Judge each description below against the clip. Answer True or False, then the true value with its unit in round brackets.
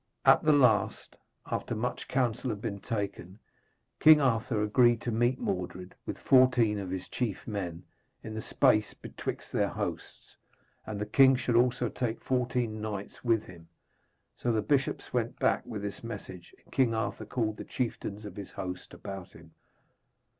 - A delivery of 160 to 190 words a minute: True (165 wpm)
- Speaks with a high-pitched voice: False (110 Hz)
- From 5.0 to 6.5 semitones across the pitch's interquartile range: False (3.6 semitones)